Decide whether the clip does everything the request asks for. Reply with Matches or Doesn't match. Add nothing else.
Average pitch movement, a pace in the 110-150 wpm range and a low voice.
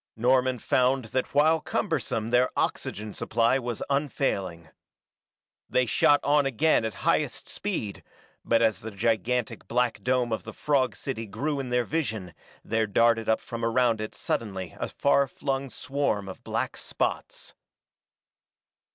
Matches